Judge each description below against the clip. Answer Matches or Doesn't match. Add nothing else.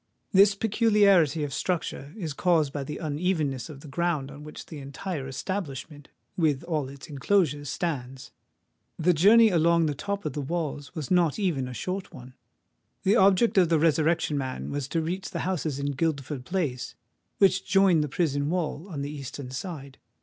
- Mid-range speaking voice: Matches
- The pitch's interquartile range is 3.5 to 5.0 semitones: Matches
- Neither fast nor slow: Matches